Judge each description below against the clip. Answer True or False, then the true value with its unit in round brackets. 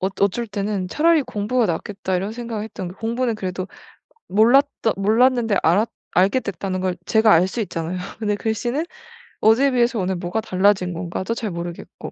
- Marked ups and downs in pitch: False (3.9 semitones)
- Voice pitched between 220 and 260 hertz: False (210 Hz)